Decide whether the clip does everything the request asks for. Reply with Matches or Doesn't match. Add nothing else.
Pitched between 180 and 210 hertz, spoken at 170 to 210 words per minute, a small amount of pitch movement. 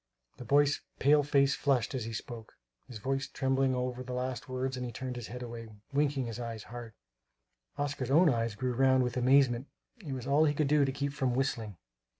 Doesn't match